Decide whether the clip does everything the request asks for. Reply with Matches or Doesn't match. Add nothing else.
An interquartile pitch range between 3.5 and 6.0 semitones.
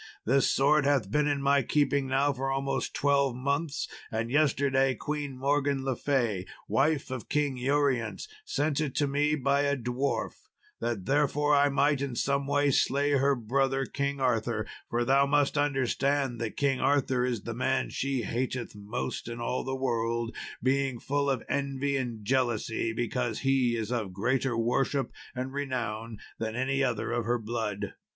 Doesn't match